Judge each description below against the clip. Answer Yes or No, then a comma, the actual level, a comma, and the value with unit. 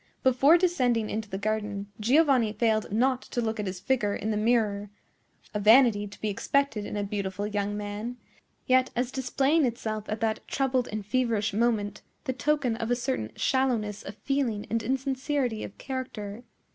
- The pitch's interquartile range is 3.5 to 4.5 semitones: Yes, average, 3.8 semitones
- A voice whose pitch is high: Yes, high, 225 Hz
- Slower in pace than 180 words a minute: Yes, average, 170 wpm